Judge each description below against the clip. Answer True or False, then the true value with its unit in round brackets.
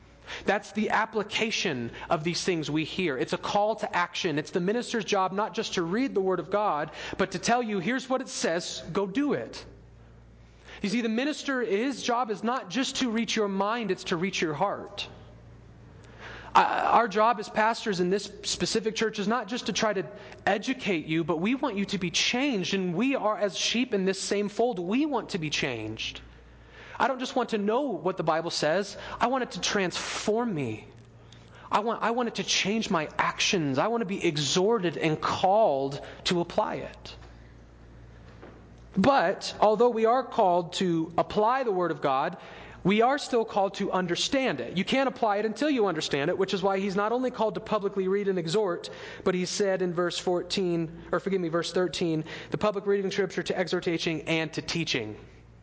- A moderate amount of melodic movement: True (4.5 semitones)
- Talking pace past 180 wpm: True (200 wpm)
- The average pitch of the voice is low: False (195 Hz)